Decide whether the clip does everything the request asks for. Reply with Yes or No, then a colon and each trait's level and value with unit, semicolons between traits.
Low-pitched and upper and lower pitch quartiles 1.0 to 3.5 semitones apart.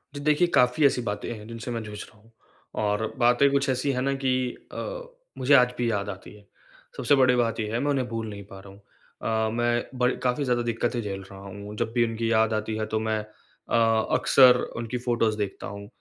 Yes: low, 115 Hz; average, 2.7 semitones